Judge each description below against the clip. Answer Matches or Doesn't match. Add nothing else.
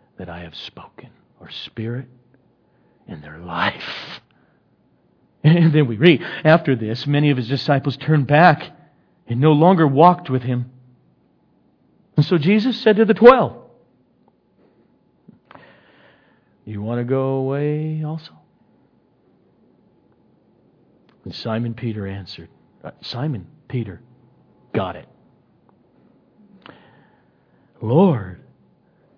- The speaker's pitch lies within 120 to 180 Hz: Matches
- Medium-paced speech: Doesn't match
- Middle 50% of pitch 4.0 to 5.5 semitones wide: Matches